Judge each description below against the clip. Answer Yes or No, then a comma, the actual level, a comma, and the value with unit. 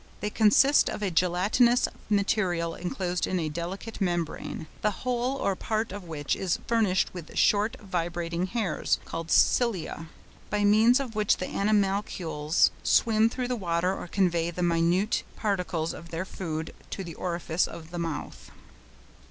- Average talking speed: Yes, average, 150 wpm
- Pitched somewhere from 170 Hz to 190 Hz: Yes, medium, 185 Hz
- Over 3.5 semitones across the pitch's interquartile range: Yes, average, 3.9 semitones